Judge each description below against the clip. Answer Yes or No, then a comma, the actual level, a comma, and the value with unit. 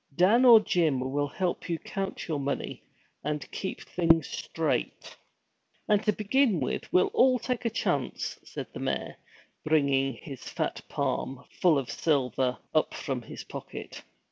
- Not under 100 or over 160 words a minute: Yes, average, 150 wpm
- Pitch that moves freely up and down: Yes, wide, 6.5 semitones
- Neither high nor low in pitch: Yes, medium, 160 Hz